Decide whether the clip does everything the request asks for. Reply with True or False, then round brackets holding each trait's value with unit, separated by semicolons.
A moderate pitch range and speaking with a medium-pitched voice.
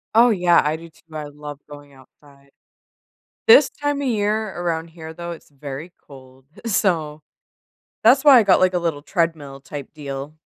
True (4.2 semitones; 160 Hz)